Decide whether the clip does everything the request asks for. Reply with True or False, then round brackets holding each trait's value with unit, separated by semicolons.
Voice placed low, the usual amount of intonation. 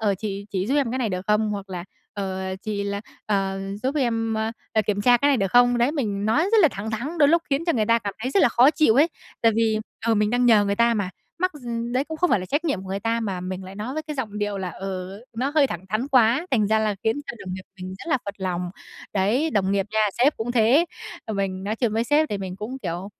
False (220 Hz; 4.6 semitones)